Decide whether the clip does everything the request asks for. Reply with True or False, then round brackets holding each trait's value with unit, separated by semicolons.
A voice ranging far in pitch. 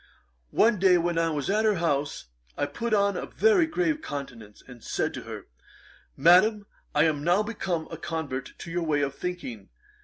True (6.3 semitones)